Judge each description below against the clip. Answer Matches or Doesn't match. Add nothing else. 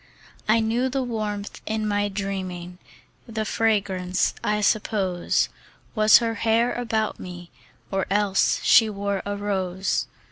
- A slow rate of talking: Matches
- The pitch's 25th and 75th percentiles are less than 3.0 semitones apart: Matches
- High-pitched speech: Matches